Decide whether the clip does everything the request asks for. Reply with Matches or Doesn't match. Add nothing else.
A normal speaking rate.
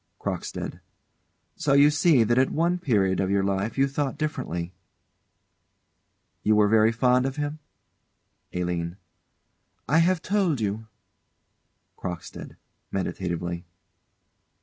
Doesn't match